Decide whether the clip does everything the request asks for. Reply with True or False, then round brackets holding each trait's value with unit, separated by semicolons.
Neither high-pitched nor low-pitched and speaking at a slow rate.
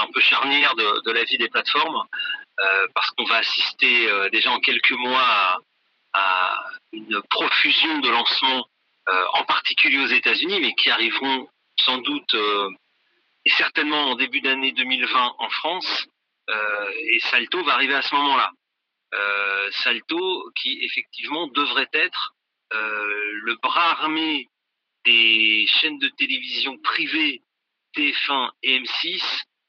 True (145 Hz; 140 wpm)